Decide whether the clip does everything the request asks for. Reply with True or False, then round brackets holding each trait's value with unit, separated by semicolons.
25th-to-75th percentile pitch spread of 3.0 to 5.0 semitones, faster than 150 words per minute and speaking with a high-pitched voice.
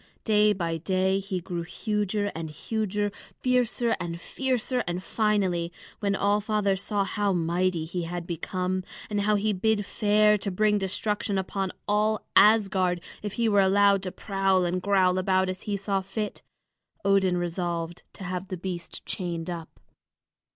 False (2.4 semitones; 160 wpm; 195 Hz)